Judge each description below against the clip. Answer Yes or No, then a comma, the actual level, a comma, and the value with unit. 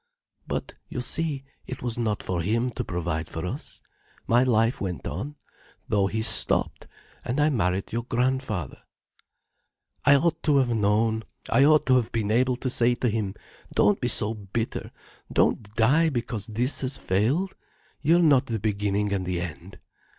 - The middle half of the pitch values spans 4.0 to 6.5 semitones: Yes, average, 4.4 semitones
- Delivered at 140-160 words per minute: No, average, 170 wpm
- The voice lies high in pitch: No, low, 115 Hz